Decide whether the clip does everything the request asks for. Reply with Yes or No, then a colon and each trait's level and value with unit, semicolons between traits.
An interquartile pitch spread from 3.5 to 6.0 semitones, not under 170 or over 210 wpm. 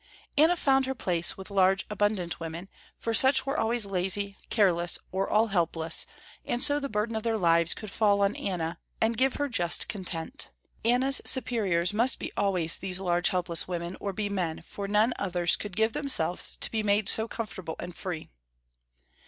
Yes: average, 4.3 semitones; average, 180 wpm